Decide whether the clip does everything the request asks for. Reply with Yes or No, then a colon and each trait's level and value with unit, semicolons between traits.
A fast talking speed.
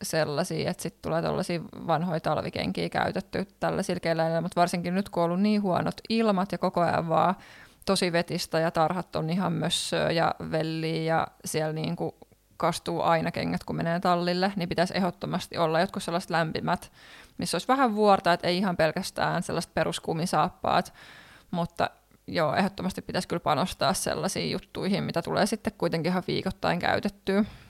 Yes: fast, 165 wpm